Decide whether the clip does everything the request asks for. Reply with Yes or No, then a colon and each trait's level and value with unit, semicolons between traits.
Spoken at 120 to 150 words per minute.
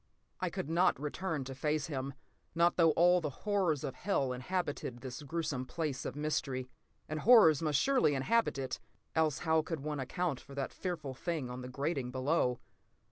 No: average, 180 wpm